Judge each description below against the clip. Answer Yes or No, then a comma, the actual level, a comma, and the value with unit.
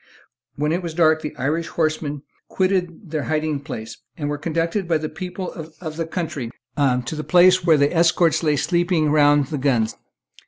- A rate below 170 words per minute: No, average, 180 wpm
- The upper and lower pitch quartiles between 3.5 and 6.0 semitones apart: No, average, 2.8 semitones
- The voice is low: No, medium, 155 Hz